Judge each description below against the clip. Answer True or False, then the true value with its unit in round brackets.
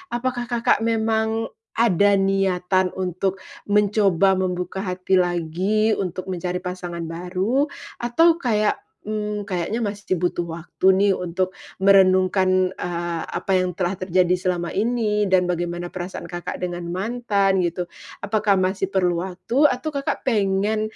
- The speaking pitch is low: False (190 Hz)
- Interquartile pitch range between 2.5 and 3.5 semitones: True (2.9 semitones)